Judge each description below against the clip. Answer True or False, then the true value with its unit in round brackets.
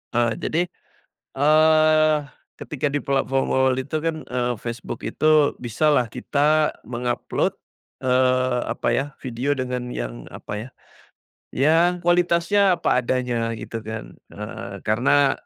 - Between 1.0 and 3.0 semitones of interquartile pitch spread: False (4.1 semitones)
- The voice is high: False (130 Hz)